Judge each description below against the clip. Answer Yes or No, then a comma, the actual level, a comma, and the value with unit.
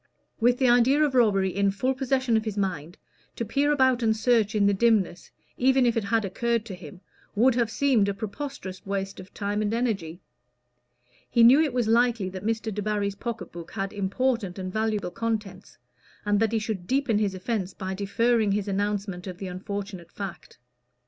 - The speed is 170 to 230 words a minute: Yes, average, 190 wpm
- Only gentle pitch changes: No, average, 3.4 semitones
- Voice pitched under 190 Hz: No, high, 215 Hz